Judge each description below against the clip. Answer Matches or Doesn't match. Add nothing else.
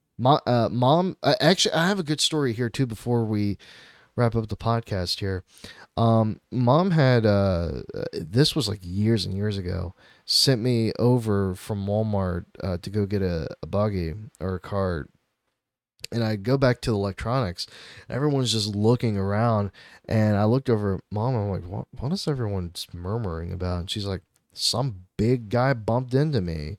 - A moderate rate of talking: Matches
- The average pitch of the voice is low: Matches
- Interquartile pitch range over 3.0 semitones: Matches